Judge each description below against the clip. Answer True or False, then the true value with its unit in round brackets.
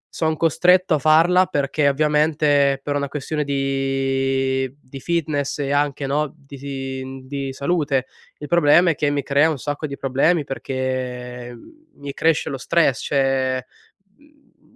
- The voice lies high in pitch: False (140 Hz)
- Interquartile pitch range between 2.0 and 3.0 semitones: True (2.4 semitones)